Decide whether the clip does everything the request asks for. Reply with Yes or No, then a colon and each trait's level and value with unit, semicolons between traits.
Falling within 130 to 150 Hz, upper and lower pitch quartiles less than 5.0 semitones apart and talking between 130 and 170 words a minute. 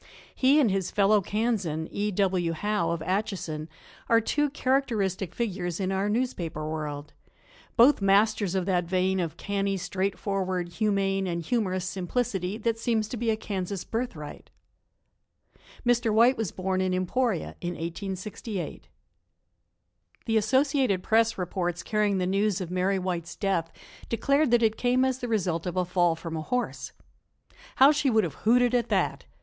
No: high, 195 Hz; average, 4.0 semitones; average, 155 wpm